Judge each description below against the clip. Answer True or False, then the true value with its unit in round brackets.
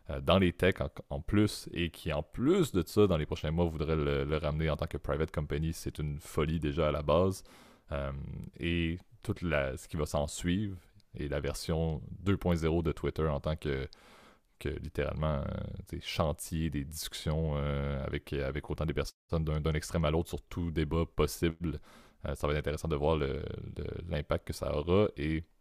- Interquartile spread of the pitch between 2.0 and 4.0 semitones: True (2.7 semitones)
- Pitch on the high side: False (80 Hz)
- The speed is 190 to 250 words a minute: True (195 wpm)